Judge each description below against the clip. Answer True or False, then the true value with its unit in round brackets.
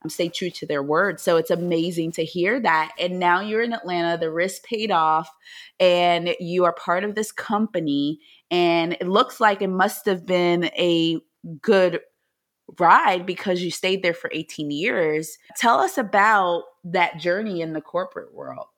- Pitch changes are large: False (2.4 semitones)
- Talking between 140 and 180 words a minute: True (175 wpm)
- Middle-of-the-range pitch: True (175 Hz)